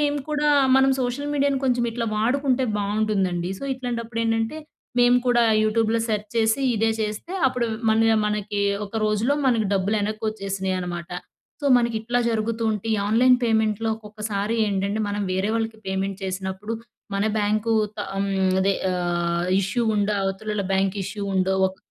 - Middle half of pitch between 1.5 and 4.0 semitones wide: Yes, average, 2.9 semitones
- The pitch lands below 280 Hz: Yes, high, 215 Hz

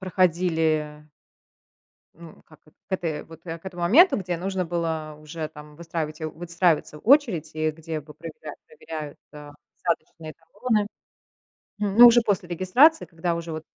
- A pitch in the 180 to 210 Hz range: No, medium, 165 Hz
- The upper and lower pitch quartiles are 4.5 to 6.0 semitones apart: No, average, 3.1 semitones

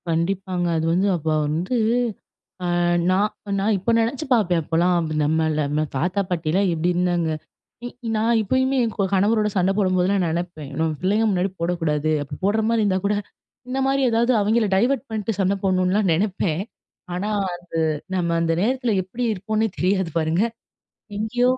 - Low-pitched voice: No, high, 190 Hz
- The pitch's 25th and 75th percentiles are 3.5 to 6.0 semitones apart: Yes, average, 4.0 semitones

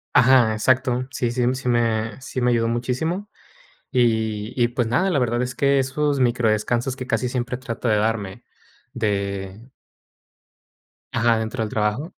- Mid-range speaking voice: No, low, 120 Hz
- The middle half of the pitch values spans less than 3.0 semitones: Yes, narrow, 2.5 semitones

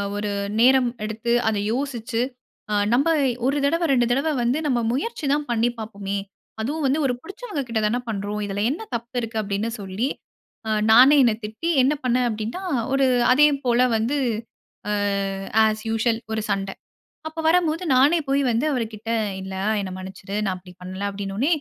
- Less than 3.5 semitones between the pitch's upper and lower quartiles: No, average, 4.5 semitones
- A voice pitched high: Yes, high, 235 Hz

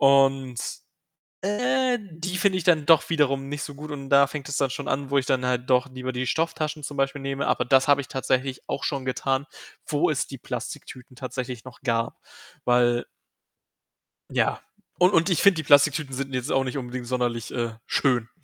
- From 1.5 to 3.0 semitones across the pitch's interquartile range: Yes, average, 2.7 semitones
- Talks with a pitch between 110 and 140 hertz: Yes, low, 135 Hz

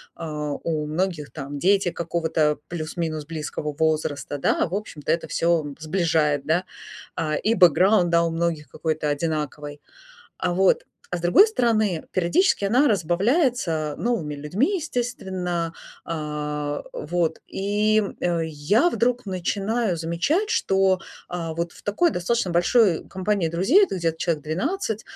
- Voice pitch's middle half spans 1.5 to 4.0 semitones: No, average, 4.6 semitones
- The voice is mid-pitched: Yes, medium, 170 Hz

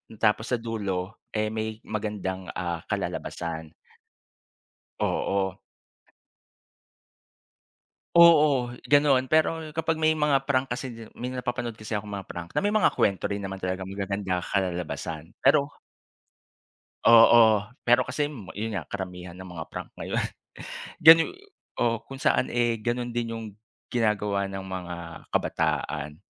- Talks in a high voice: No, low, 110 Hz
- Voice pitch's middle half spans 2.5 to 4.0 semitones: No, average, 4.8 semitones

